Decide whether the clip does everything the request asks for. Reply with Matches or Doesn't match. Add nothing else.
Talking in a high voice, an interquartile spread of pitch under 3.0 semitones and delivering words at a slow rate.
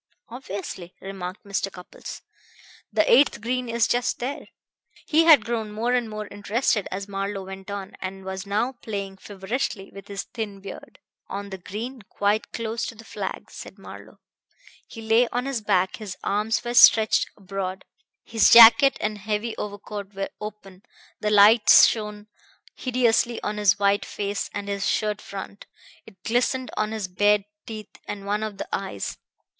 Doesn't match